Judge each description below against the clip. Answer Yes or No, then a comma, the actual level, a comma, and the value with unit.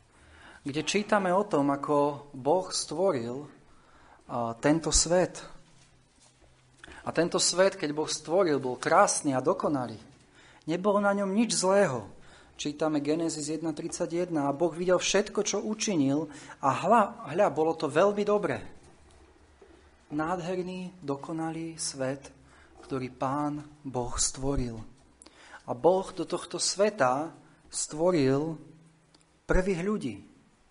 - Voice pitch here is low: No, medium, 160 Hz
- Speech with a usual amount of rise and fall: Yes, average, 4.0 semitones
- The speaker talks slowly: Yes, slow, 105 wpm